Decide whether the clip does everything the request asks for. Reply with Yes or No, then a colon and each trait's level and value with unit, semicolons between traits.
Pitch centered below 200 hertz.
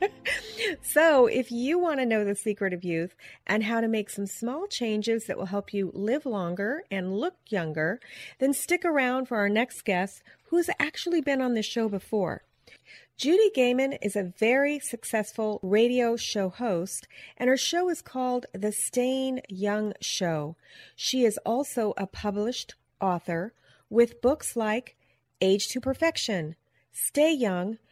No: high, 230 Hz